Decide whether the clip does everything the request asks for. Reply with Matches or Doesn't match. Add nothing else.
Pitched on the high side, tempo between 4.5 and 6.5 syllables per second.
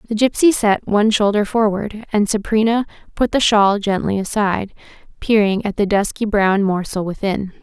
Matches